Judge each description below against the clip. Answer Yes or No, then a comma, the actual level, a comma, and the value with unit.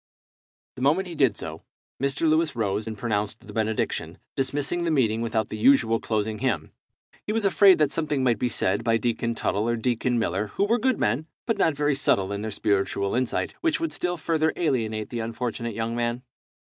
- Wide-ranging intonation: Yes, wide, 5.9 semitones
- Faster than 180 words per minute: Yes, average, 200 wpm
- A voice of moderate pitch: No, low, 120 Hz